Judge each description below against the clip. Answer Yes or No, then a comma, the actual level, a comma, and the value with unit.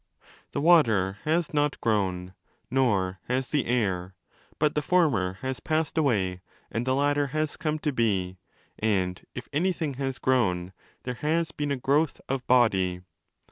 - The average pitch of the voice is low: Yes, low, 130 Hz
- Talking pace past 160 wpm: No, average, 140 wpm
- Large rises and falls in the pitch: Yes, wide, 7.5 semitones